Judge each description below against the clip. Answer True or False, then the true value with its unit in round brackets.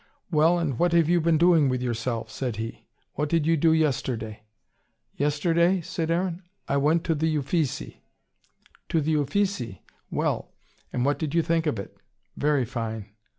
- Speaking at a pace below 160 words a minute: False (165 wpm)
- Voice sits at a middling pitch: True (150 Hz)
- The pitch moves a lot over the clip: False (4.7 semitones)